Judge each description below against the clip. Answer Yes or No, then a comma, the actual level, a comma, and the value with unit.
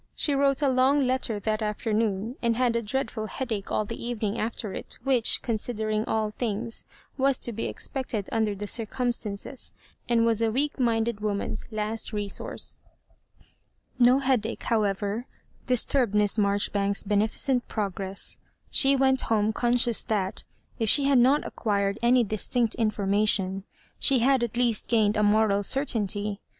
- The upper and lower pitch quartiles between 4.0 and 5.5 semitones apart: No, average, 3.0 semitones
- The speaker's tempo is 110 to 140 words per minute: No, average, 160 wpm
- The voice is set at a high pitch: Yes, high, 225 Hz